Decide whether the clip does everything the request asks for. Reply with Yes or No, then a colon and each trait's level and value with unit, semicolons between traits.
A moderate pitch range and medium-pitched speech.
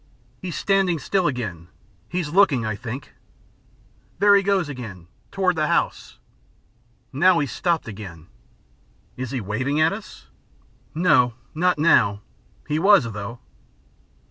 No: wide, 8.0 semitones; medium, 145 Hz